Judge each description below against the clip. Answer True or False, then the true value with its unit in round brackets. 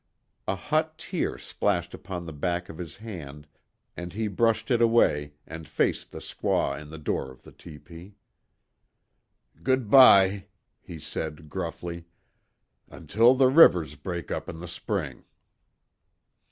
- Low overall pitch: True (90 Hz)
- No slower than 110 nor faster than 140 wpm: True (135 wpm)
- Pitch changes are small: False (5.6 semitones)